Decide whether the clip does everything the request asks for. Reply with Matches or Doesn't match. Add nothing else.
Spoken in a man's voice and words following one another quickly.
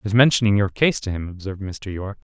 Matches